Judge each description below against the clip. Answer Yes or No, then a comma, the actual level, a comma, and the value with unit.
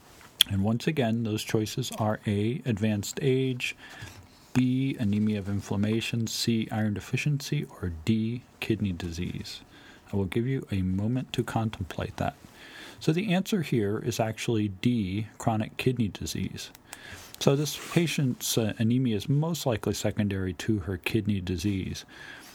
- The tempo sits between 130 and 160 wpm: Yes, average, 140 wpm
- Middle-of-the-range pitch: No, low, 110 Hz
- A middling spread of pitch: Yes, average, 3.6 semitones